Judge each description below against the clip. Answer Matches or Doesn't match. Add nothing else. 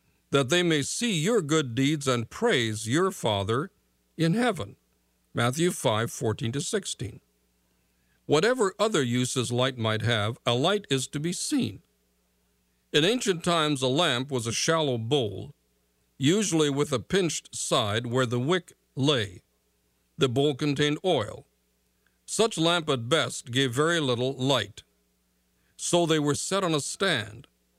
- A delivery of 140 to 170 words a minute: Matches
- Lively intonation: Matches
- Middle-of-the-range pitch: Doesn't match